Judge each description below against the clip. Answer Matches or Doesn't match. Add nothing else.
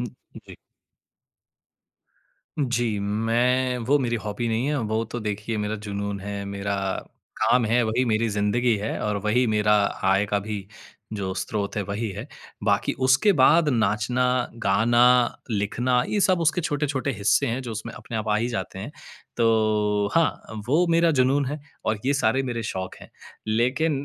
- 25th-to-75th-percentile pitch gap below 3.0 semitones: Doesn't match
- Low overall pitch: Matches